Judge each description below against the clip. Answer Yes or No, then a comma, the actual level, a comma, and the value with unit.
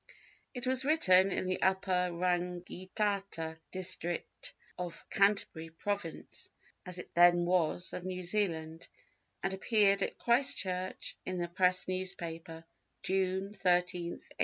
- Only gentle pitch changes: Yes, narrow, 1.9 semitones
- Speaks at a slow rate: Yes, slow, 120 wpm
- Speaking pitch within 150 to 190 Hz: Yes, medium, 185 Hz